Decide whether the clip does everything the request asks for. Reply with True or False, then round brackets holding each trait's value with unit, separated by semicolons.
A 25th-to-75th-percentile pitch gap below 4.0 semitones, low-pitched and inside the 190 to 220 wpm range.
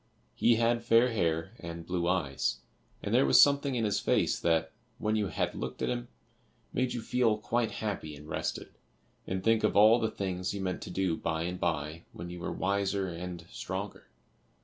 False (5.0 semitones; 95 Hz; 195 wpm)